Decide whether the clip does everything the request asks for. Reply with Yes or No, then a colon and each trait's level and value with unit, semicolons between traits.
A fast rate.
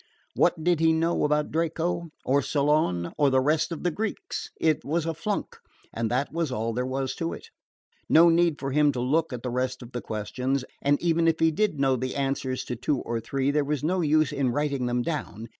Yes: fast, 225 wpm